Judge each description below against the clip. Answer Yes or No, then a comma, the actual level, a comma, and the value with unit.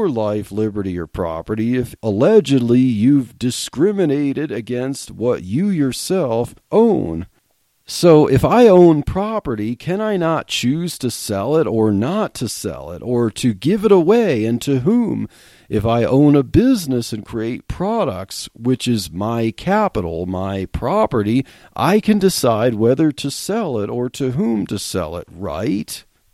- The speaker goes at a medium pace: Yes, average, 150 wpm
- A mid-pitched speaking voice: No, low, 125 Hz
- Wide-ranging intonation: Yes, wide, 6.7 semitones